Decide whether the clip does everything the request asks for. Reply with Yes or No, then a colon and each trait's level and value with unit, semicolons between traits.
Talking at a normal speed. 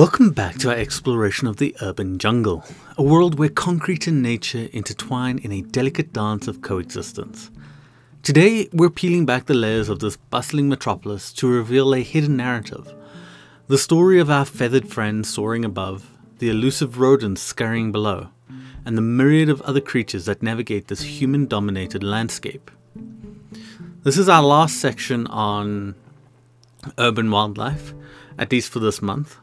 Yes: average, 155 wpm